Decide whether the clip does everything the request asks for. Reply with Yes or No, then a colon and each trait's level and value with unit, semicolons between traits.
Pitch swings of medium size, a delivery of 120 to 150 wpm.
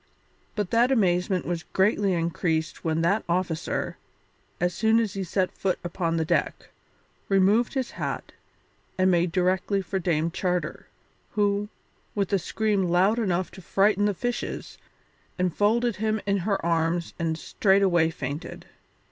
Yes: average, 3.1 semitones; average, 140 wpm